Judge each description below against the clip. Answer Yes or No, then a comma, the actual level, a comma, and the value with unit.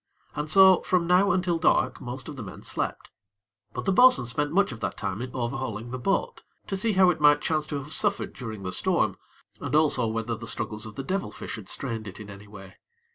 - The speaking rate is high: Yes, fast, 230 wpm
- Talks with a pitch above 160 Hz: No, low, 135 Hz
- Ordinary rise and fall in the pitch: No, wide, 8.1 semitones